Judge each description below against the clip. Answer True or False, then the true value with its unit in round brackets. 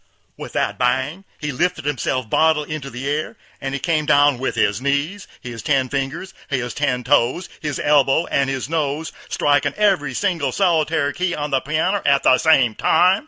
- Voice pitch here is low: False (145 Hz)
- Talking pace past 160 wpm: True (180 wpm)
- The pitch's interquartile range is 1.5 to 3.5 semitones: True (3.1 semitones)